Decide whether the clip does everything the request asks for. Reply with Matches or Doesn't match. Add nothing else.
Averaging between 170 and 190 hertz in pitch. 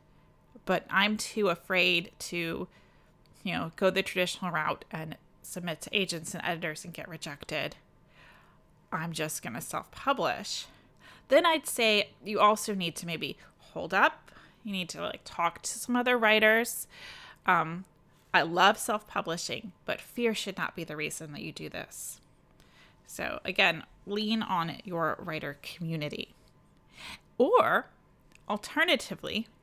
Matches